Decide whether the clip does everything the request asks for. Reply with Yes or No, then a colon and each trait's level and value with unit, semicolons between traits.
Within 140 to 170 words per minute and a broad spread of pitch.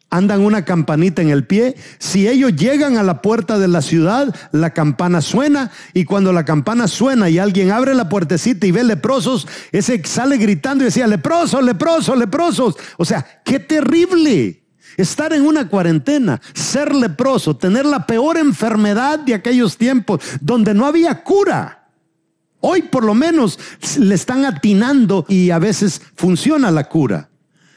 Yes: average, 160 wpm; wide, 6.6 semitones